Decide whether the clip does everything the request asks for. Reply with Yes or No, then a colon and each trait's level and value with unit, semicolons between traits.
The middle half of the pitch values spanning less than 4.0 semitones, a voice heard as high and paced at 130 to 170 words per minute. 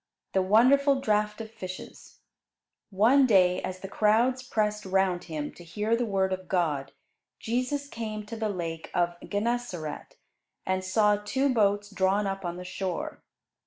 Yes: average, 3.4 semitones; high, 205 Hz; average, 160 wpm